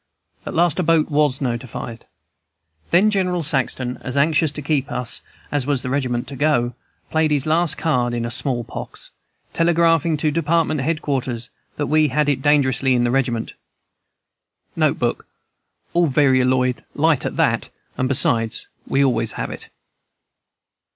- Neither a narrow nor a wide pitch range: Yes, average, 3.6 semitones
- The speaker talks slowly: No, average, 150 wpm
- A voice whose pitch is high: No, medium, 140 Hz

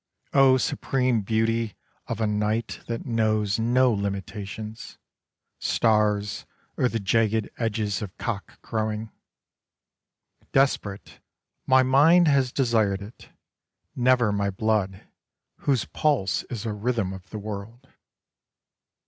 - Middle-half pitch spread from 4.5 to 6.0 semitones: No, average, 3.1 semitones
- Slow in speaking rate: Yes, slow, 115 wpm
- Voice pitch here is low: Yes, low, 110 Hz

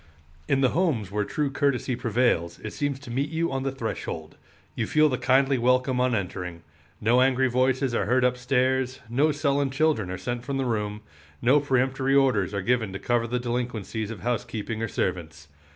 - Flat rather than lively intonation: No, average, 3.3 semitones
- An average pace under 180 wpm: No, average, 190 wpm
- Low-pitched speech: Yes, low, 125 Hz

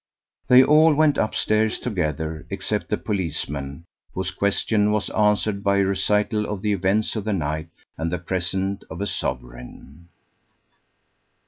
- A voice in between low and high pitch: No, low, 100 Hz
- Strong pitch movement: No, average, 4.4 semitones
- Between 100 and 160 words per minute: Yes, average, 140 wpm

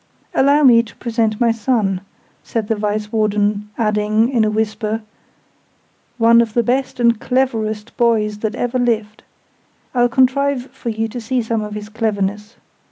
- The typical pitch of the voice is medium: No, high, 225 Hz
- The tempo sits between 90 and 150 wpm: No, average, 160 wpm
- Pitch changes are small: Yes, narrow, 2.3 semitones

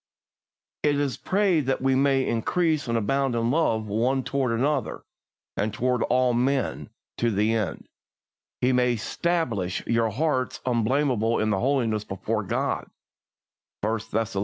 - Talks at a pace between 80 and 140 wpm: Yes, slow, 135 wpm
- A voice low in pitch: Yes, low, 125 Hz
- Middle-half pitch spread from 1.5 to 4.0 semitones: Yes, average, 3.6 semitones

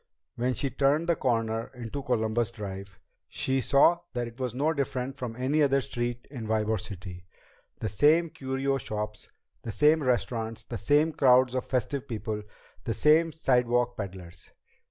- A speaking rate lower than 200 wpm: Yes, average, 155 wpm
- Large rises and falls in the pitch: No, average, 3.7 semitones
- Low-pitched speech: Yes, low, 125 Hz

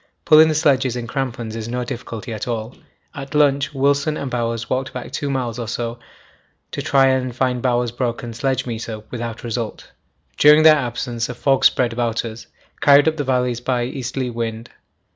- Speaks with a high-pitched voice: No, low, 125 Hz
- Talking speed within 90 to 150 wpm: No, average, 180 wpm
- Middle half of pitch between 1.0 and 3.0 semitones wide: Yes, narrow, 2.5 semitones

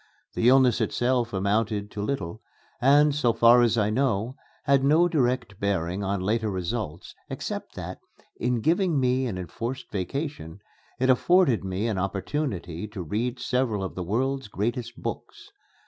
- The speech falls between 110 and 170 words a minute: Yes, average, 150 wpm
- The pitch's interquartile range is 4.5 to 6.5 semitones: Yes, average, 4.8 semitones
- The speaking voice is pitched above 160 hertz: No, low, 115 Hz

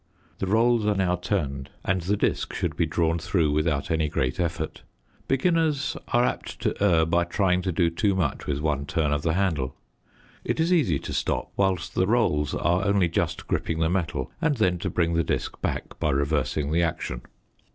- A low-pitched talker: Yes, very low, 85 Hz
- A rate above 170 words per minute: Yes, average, 195 wpm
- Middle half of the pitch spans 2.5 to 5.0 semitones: Yes, average, 4.1 semitones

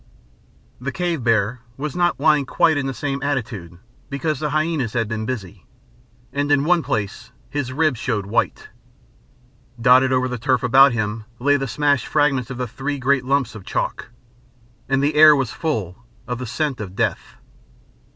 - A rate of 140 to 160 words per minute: No, average, 170 wpm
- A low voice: Yes, low, 130 Hz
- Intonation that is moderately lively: Yes, average, 3.7 semitones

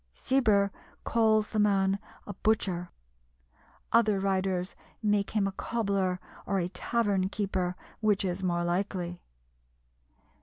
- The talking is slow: Yes, slow, 115 wpm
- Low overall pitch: No, high, 195 Hz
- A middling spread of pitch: No, narrow, 2.2 semitones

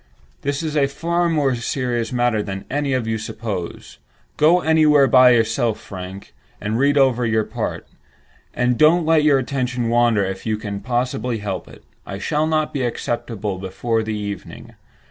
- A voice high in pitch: No, low, 120 Hz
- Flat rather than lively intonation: No, average, 4.7 semitones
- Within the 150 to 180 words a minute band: Yes, average, 165 wpm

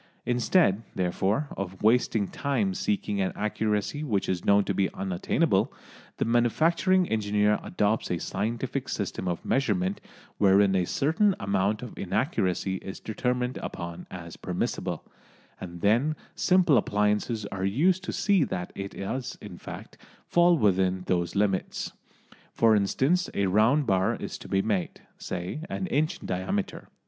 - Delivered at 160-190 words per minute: No, average, 145 wpm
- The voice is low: Yes, low, 105 Hz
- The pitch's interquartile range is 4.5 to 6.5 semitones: Yes, wide, 5.6 semitones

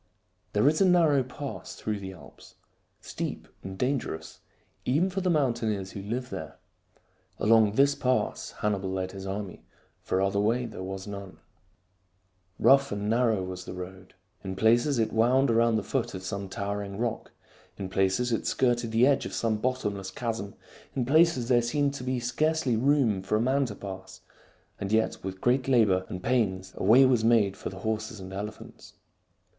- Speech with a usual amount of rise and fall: Yes, average, 4.6 semitones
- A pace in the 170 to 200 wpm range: Yes, average, 175 wpm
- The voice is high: No, low, 110 Hz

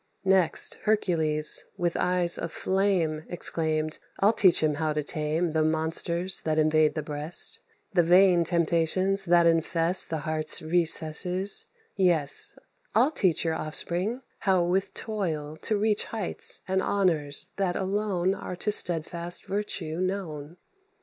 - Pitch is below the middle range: No, medium, 170 Hz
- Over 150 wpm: No, slow, 135 wpm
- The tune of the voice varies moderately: Yes, average, 3.3 semitones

